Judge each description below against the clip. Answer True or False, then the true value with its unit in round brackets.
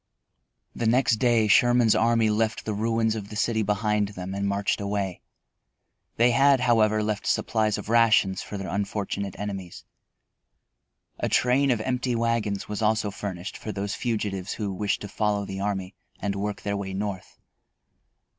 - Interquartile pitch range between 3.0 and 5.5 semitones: False (2.4 semitones)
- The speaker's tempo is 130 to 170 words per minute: True (160 wpm)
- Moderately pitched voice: False (105 Hz)